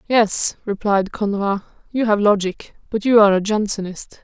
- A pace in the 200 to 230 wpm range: No, average, 155 wpm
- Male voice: No, female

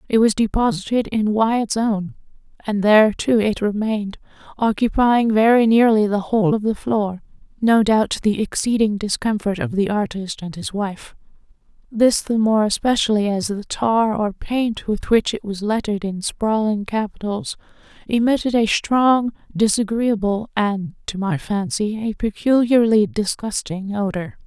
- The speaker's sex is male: No, female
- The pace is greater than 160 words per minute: No, average, 140 wpm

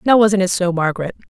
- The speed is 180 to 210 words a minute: No, fast, 225 wpm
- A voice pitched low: No, high, 190 Hz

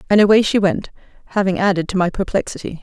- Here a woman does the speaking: Yes, female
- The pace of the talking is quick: No, average, 190 wpm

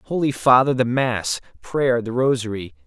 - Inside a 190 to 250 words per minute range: No, slow, 125 wpm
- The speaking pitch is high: No, low, 120 Hz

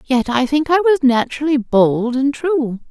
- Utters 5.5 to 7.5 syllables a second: No, 4.4 syllables/s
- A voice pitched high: Yes, very high, 270 Hz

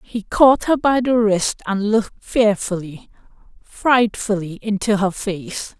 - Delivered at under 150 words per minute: Yes, slow, 135 wpm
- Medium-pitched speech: No, high, 210 Hz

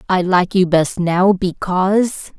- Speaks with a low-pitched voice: No, medium, 185 Hz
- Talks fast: No, average, 150 wpm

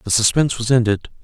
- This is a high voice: No, low, 115 Hz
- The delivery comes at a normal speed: Yes, average, 195 wpm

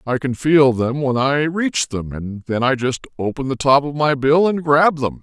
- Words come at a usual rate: No, fast, 240 wpm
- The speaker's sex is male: Yes, male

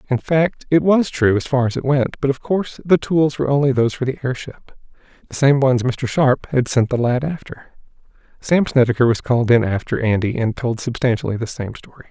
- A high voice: No, low, 130 Hz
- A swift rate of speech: Yes, fast, 220 wpm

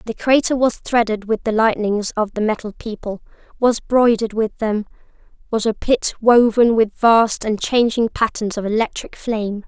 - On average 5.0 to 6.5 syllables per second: No, 4.7 syllables/s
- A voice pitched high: Yes, high, 220 Hz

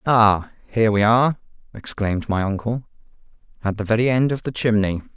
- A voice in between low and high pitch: No, low, 110 Hz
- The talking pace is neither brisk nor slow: Yes, average, 165 wpm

